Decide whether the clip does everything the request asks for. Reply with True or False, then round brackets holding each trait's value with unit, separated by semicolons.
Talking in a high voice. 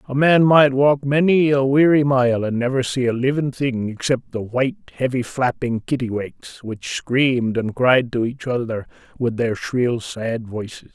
False (125 Hz)